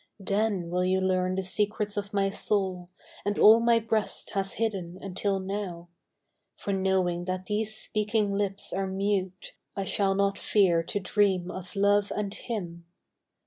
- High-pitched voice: Yes, high, 195 Hz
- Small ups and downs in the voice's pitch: Yes, narrow, 1.9 semitones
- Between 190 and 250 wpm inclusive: No, average, 155 wpm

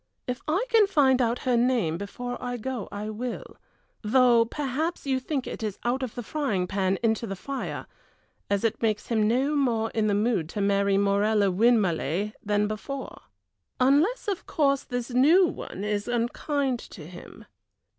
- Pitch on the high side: Yes, high, 235 Hz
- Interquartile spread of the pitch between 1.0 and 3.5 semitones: No, average, 4.3 semitones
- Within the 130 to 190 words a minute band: Yes, average, 170 wpm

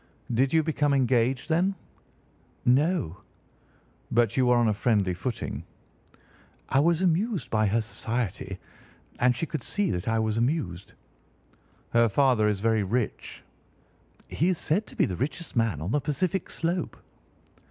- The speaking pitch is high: No, low, 125 Hz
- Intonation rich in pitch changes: Yes, wide, 6.4 semitones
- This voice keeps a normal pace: Yes, average, 150 wpm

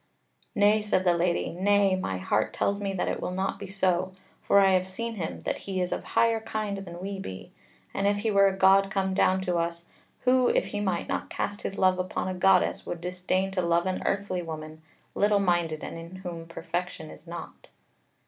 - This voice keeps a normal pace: No, fast, 215 wpm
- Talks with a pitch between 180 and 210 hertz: Yes, medium, 185 Hz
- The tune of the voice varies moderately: No, narrow, 2.2 semitones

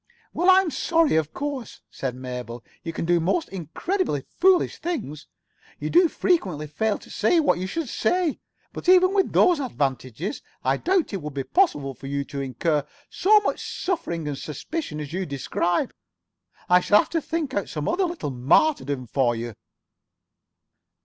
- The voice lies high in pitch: No, medium, 180 Hz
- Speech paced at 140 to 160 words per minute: No, average, 170 wpm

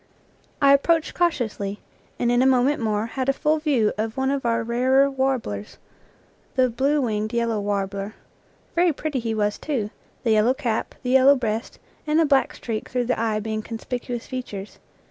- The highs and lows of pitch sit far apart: No, average, 3.8 semitones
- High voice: Yes, high, 245 Hz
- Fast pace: No, average, 175 wpm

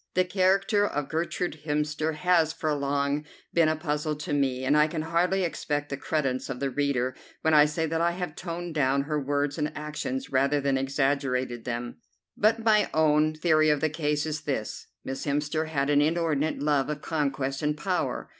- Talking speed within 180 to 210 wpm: Yes, average, 190 wpm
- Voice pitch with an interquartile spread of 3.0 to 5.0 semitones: No, narrow, 2.4 semitones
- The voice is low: No, medium, 150 Hz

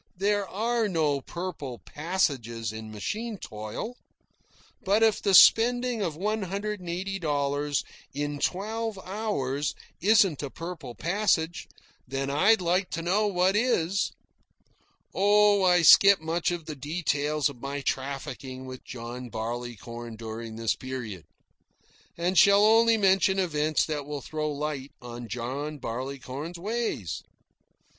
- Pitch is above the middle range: No, medium, 160 Hz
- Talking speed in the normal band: No, slow, 130 wpm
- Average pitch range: No, wide, 6.9 semitones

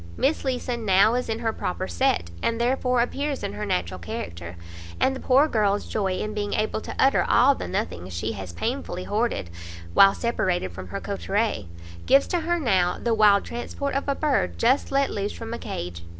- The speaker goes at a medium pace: Yes, average, 195 wpm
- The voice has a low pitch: No, high, 215 Hz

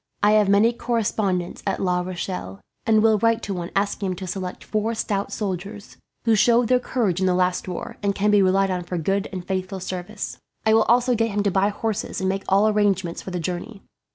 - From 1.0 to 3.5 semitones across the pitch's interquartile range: Yes, average, 2.8 semitones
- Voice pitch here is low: No, high, 200 Hz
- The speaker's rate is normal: No, fast, 220 wpm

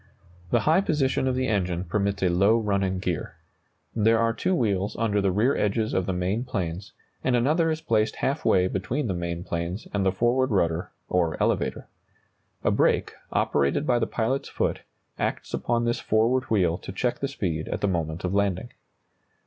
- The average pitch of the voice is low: Yes, low, 105 Hz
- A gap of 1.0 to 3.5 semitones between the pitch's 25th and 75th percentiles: No, average, 4.8 semitones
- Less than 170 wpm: No, average, 185 wpm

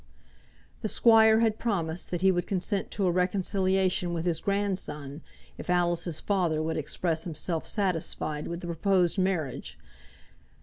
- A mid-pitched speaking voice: Yes, medium, 180 Hz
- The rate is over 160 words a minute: No, average, 140 wpm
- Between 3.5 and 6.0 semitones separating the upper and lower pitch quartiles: No, average, 3.0 semitones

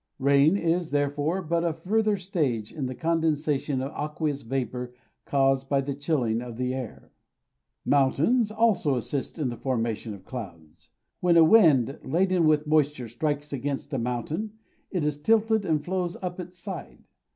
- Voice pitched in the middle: Yes, medium, 150 Hz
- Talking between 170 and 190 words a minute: No, average, 160 wpm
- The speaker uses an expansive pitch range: No, average, 4.6 semitones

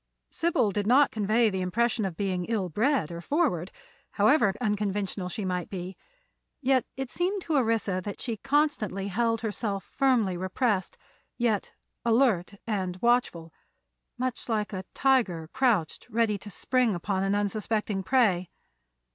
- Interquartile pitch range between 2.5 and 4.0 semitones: No, average, 4.4 semitones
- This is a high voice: Yes, high, 210 Hz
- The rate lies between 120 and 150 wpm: Yes, average, 140 wpm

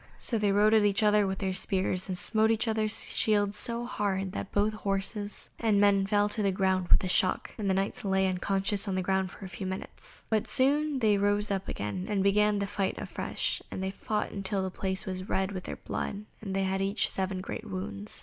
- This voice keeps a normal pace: No, fast, 225 wpm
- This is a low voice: No, high, 195 Hz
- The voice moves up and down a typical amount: No, narrow, 1.7 semitones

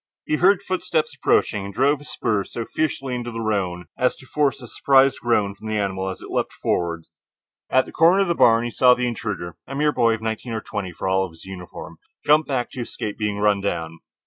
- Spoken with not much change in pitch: No, wide, 5.6 semitones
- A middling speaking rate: No, fast, 230 wpm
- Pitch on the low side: Yes, low, 115 Hz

